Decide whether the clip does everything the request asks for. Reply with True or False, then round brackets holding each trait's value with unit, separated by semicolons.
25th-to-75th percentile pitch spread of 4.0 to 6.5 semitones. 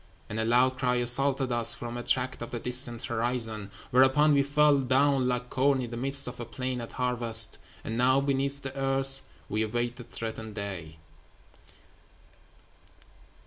False (2.4 semitones)